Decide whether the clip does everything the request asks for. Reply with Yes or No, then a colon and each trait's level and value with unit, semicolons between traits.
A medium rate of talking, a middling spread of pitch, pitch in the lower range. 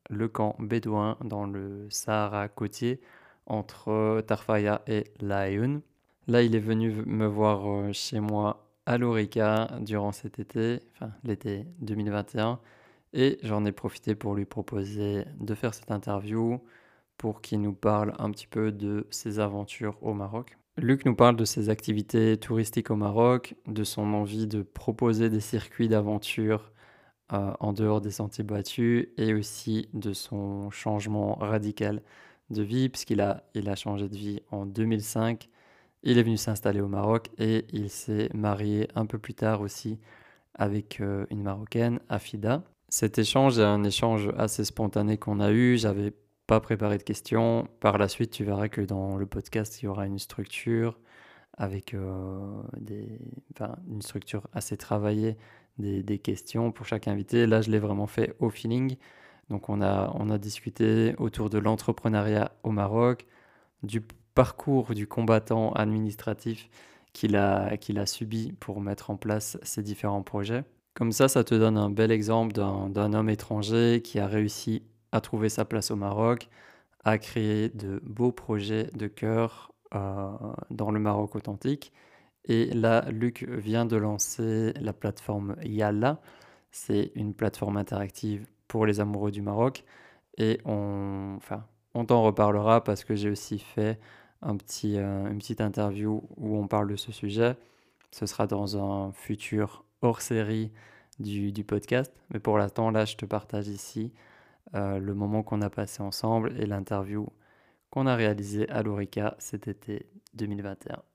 No: average, 160 wpm; narrow, 1.7 semitones; low, 110 Hz